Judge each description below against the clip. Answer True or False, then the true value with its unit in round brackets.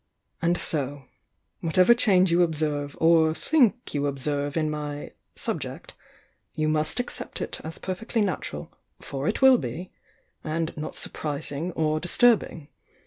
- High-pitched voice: False (160 Hz)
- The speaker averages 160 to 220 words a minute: False (145 wpm)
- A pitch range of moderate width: True (3.7 semitones)